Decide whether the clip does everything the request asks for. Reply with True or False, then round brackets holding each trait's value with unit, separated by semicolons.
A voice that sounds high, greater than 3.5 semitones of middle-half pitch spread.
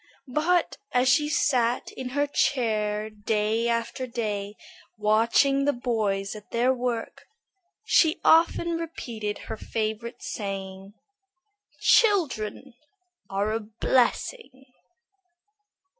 True (235 Hz; 4.4 semitones)